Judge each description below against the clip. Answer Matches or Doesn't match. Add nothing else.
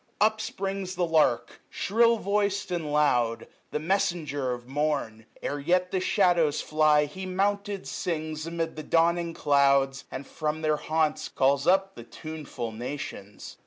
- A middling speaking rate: Matches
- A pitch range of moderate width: Matches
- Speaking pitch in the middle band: Matches